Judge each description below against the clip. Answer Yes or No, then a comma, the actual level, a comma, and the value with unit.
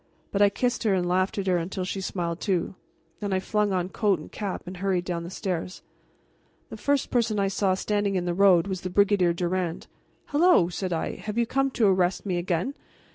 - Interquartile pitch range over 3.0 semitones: No, narrow, 2.5 semitones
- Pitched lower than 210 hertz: Yes, high, 190 Hz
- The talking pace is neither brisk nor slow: No, fast, 215 wpm